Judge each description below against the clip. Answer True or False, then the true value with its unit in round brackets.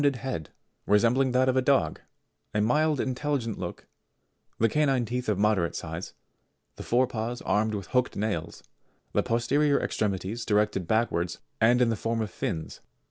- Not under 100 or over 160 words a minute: False (170 wpm)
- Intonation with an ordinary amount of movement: True (3.8 semitones)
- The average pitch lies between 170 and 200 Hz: False (115 Hz)